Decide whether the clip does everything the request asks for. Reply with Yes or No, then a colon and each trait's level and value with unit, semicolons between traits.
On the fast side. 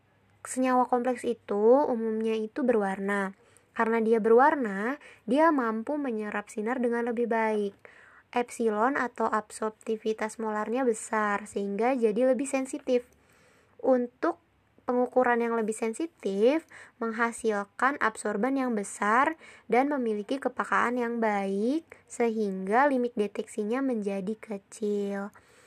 No: average, 105 wpm